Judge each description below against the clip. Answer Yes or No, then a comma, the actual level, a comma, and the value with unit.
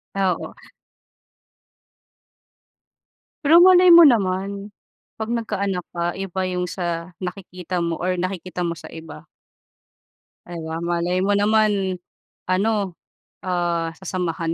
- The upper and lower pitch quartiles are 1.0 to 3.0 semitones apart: Yes, narrow, 2.5 semitones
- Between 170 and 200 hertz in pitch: Yes, medium, 185 Hz